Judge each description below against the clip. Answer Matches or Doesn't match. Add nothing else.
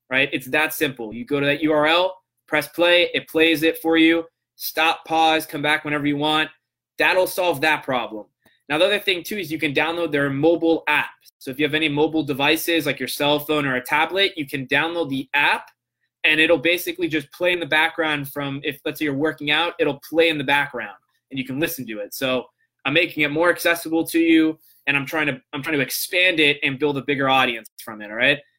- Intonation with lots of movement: Doesn't match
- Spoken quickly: Matches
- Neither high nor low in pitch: Matches